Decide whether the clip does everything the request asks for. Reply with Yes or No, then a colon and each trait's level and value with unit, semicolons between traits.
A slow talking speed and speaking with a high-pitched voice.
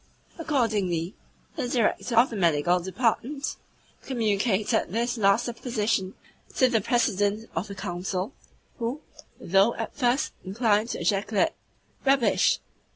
Yes: slow, 120 wpm; high, 220 Hz